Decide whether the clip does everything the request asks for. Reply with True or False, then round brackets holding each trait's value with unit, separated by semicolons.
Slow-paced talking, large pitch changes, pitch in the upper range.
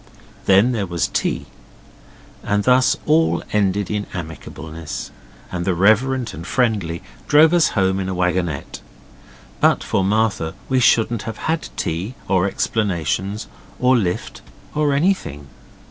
False (130 wpm; 6.0 semitones; 100 Hz)